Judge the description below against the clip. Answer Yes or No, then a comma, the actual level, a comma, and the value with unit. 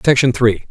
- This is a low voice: Yes, low, 120 Hz